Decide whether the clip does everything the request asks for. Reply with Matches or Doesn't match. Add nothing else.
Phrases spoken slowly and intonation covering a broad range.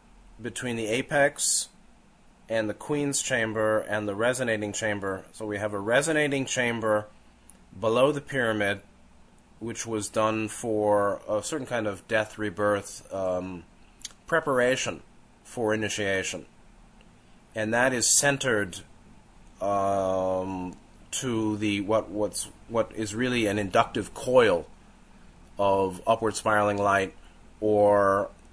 Doesn't match